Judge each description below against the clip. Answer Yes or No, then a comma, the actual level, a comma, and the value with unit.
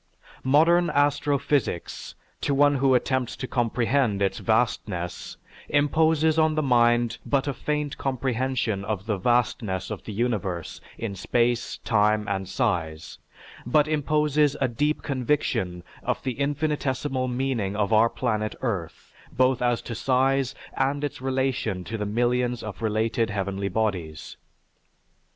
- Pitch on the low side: Yes, low, 120 Hz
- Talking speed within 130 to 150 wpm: Yes, slow, 135 wpm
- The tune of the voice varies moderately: Yes, average, 4.5 semitones